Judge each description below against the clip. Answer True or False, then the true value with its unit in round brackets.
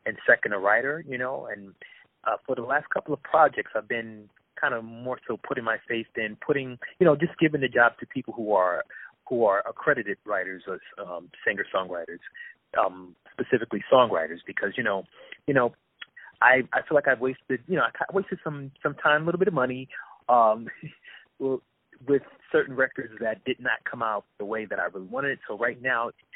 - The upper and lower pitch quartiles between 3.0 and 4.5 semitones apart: True (4.2 semitones)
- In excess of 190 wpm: True (200 wpm)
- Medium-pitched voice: False (130 Hz)